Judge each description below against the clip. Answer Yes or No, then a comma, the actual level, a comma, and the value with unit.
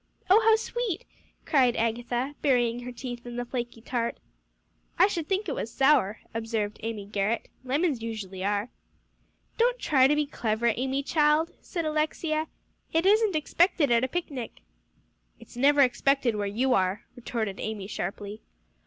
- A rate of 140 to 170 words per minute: Yes, average, 155 wpm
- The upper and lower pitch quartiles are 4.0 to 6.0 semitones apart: Yes, average, 5.2 semitones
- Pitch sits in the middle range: No, very high, 250 Hz